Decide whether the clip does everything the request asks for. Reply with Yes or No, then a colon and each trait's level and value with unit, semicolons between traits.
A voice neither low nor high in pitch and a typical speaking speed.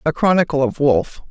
Yes: medium, 155 Hz; average, 185 wpm